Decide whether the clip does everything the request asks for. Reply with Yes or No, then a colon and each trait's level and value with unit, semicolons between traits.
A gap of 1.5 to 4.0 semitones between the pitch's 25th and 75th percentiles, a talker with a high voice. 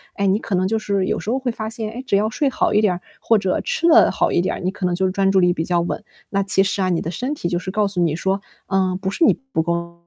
Yes: average, 3.0 semitones; high, 195 Hz